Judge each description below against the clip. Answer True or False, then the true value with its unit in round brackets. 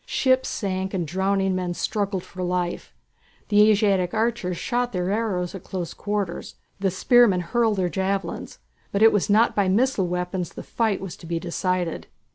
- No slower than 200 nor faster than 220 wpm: False (170 wpm)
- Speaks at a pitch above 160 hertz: True (190 Hz)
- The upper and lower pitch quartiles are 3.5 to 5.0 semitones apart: False (2.8 semitones)